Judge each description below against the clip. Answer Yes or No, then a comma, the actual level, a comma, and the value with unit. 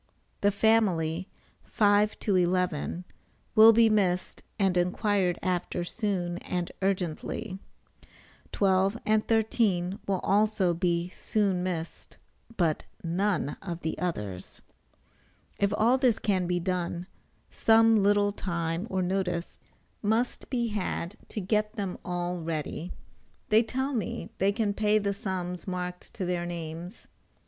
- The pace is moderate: No, slow, 125 wpm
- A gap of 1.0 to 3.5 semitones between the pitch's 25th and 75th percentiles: Yes, average, 3.1 semitones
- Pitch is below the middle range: No, high, 190 Hz